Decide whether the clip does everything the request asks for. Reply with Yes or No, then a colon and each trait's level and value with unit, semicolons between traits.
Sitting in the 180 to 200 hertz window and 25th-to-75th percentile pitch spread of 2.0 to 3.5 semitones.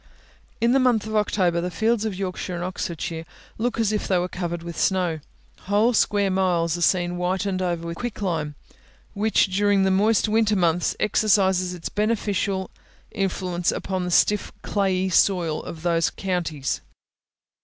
Yes: high, 190 Hz; average, 3.0 semitones